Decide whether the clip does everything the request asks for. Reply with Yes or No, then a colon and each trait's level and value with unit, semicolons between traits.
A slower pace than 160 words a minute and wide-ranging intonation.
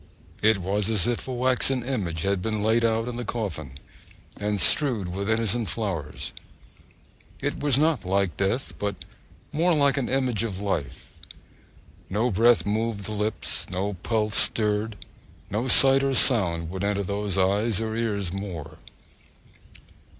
No: average, 150 wpm; average, 3.4 semitones